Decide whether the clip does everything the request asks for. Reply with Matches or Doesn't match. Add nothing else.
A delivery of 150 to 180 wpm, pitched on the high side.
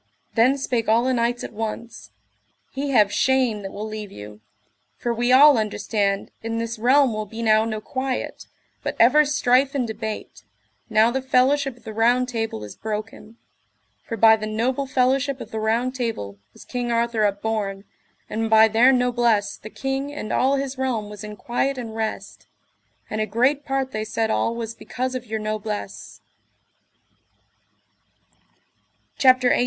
Matches